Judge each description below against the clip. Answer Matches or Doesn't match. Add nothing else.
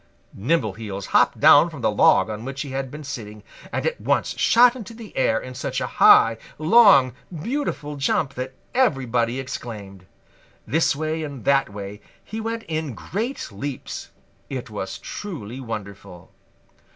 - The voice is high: Doesn't match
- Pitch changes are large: Matches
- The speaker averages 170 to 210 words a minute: Doesn't match